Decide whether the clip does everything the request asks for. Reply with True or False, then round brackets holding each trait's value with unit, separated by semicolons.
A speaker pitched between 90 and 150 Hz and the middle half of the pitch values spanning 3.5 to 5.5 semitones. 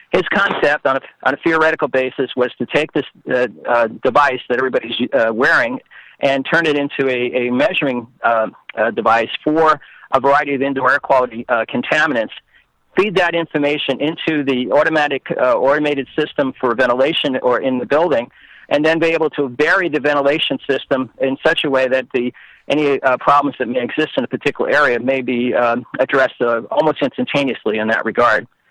False (140 Hz; 2.8 semitones)